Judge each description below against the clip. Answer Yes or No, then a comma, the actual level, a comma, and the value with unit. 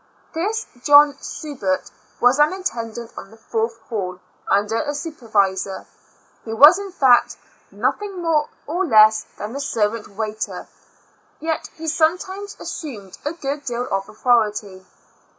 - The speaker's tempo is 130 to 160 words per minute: Yes, slow, 135 wpm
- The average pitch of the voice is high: Yes, high, 245 Hz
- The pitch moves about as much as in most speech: No, wide, 6.6 semitones